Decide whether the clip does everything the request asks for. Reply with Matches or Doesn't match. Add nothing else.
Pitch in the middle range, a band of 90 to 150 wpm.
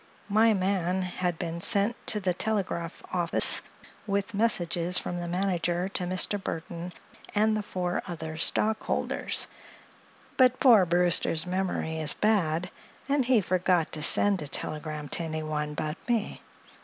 Matches